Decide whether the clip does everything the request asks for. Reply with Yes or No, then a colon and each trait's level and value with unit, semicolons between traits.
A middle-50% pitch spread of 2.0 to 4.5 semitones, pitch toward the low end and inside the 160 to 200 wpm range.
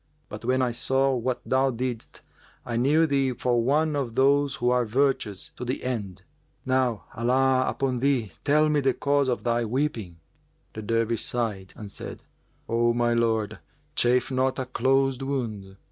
Yes: narrow, 2.5 semitones; low, 125 Hz; average, 165 wpm